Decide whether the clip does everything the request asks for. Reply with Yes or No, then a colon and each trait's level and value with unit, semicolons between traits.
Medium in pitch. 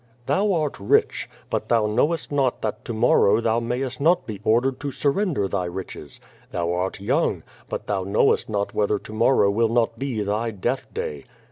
No: low, 115 Hz